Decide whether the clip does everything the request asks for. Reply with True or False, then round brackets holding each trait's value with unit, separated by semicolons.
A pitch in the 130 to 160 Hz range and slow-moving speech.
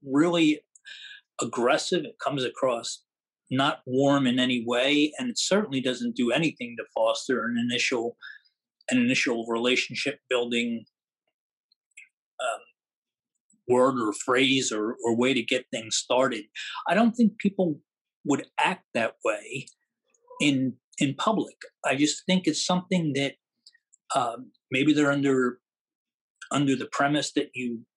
True (140 Hz; 130 wpm)